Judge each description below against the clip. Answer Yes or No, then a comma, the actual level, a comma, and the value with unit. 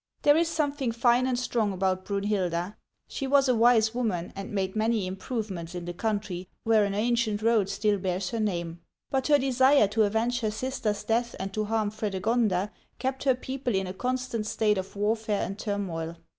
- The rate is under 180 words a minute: No, average, 190 wpm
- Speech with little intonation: No, average, 3.9 semitones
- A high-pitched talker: Yes, high, 215 Hz